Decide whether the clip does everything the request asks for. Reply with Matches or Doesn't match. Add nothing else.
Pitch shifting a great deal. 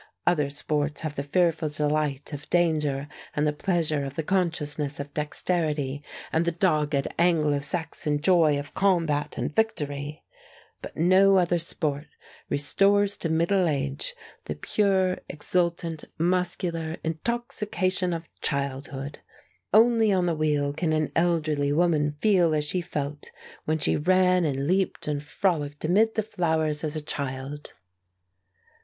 Doesn't match